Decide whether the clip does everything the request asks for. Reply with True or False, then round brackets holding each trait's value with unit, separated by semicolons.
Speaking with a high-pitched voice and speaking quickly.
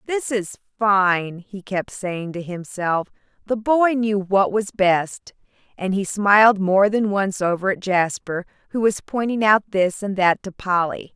False (200 Hz; 170 wpm)